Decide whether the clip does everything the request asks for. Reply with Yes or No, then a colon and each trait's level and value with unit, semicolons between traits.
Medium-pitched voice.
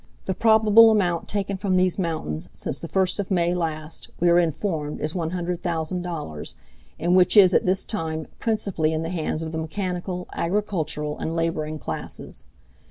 Yes: medium, 175 Hz